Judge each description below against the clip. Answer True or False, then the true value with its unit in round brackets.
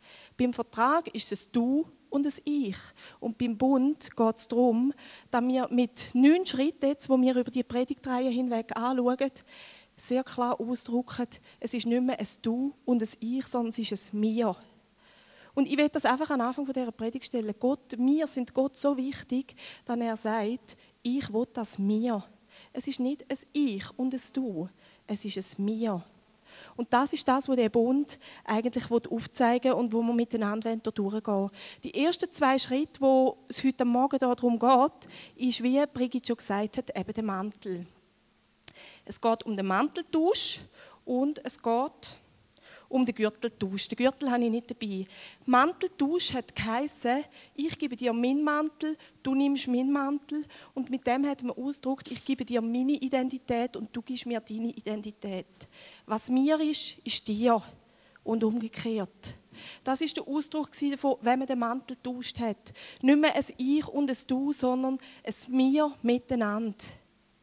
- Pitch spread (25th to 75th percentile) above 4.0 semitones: False (3.1 semitones)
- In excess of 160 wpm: True (170 wpm)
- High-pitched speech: True (250 Hz)